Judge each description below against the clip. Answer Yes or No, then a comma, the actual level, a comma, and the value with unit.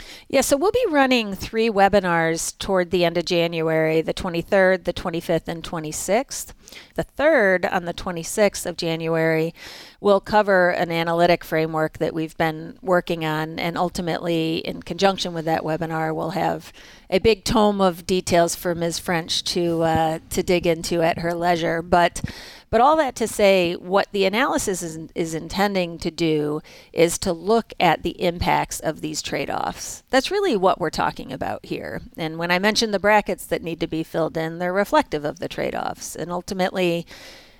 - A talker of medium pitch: Yes, medium, 175 Hz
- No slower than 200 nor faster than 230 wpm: No, average, 175 wpm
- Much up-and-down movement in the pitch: No, average, 3.0 semitones